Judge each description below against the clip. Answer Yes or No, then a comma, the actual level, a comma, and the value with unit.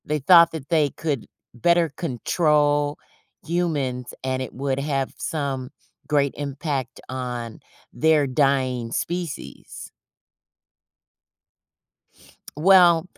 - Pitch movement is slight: No, average, 3.5 semitones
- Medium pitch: Yes, medium, 145 Hz